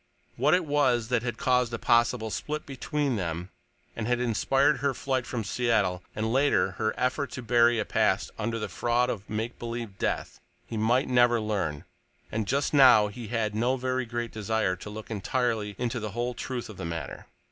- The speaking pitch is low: Yes, low, 120 Hz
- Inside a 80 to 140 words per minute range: No, average, 195 wpm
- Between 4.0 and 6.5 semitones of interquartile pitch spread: No, average, 2.8 semitones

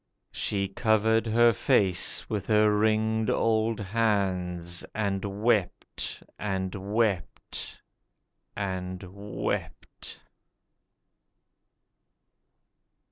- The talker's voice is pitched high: No, low, 105 Hz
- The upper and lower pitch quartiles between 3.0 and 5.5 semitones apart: No, narrow, 2.5 semitones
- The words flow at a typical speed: No, slow, 70 wpm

